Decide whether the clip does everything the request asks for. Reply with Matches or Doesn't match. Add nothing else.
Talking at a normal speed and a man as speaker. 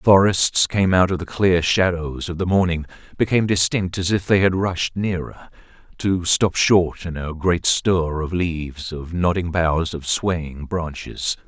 Matches